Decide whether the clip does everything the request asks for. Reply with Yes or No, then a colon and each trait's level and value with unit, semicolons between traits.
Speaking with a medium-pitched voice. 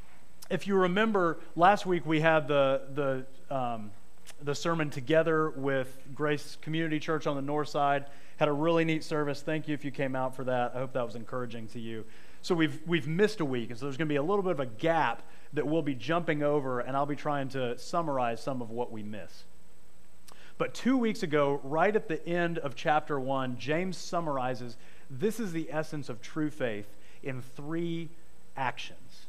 Yes: medium, 150 Hz